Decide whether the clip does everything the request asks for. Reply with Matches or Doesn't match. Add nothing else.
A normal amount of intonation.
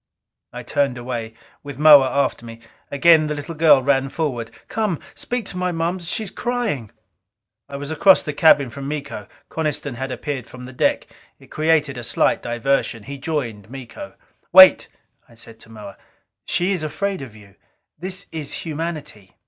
Matches